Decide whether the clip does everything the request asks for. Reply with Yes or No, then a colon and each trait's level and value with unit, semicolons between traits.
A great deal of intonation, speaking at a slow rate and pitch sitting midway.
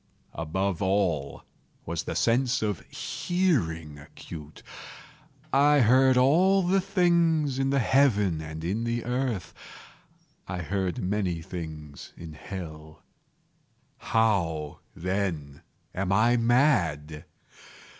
No: wide, 8.4 semitones; slow, 100 wpm; low, 100 Hz